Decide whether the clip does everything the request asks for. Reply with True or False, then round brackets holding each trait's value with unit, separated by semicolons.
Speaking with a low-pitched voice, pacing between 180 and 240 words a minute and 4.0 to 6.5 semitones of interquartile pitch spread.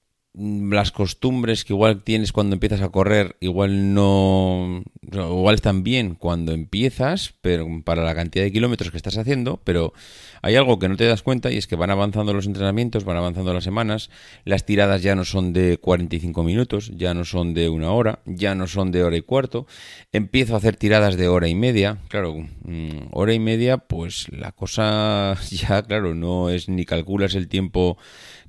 False (100 Hz; 185 wpm; 3.1 semitones)